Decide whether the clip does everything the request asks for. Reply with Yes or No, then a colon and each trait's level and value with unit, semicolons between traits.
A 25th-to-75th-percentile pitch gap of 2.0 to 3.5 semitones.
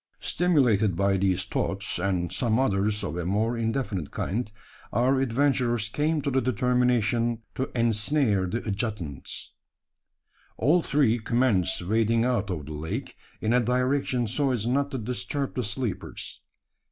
No: average, 4.3 semitones